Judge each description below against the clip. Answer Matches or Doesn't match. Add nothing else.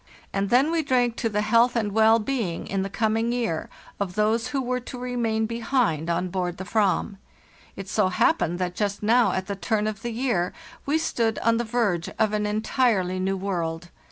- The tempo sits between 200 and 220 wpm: Matches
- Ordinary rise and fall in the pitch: Matches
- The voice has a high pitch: Matches